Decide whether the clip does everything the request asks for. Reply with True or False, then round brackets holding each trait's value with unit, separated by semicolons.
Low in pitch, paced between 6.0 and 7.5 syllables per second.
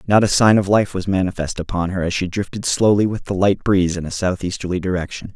True (95 Hz; 6.2 syllables/s)